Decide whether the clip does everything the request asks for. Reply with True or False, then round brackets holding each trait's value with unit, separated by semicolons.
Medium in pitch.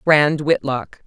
True (145 Hz)